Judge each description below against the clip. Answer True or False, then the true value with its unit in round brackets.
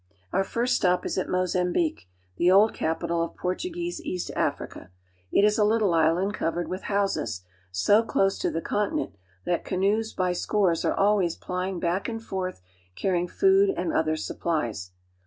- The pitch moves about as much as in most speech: True (3.6 semitones)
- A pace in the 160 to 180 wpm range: True (165 wpm)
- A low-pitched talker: False (185 Hz)